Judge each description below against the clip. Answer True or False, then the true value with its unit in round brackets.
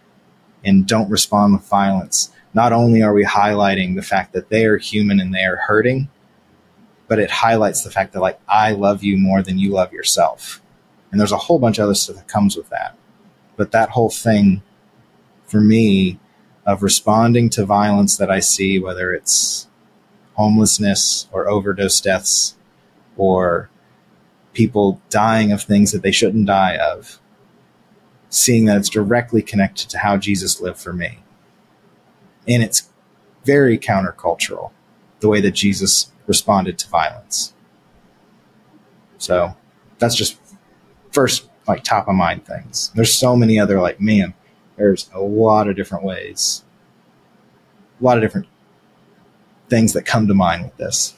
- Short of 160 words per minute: True (150 wpm)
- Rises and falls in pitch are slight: True (2.1 semitones)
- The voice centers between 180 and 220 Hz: False (105 Hz)